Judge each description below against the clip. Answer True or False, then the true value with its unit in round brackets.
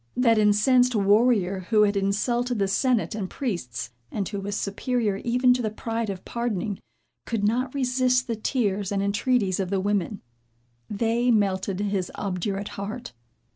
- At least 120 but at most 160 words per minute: True (155 wpm)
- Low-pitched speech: False (210 Hz)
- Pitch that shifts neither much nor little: True (3.5 semitones)